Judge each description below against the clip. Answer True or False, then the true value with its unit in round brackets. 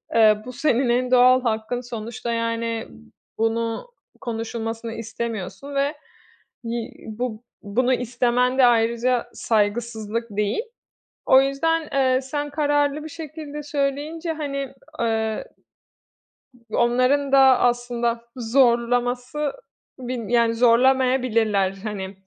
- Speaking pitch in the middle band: False (245 Hz)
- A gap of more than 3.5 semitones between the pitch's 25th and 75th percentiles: False (2.9 semitones)